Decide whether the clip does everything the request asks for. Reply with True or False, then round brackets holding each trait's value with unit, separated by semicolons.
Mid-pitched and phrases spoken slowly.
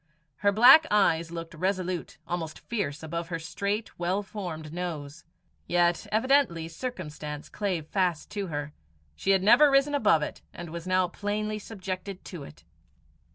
False (180 Hz; 150 wpm)